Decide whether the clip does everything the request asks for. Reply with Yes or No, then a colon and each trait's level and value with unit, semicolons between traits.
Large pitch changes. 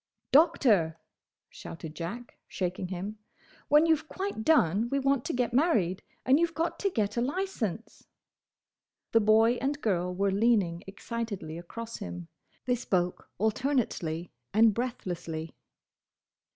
Yes: wide, 6.7 semitones